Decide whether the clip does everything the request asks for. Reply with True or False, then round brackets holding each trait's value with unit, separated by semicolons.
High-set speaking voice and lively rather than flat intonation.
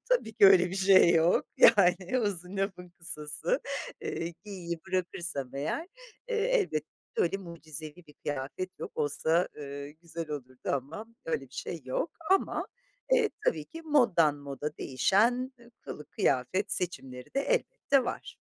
False (175 Hz; 6.2 semitones)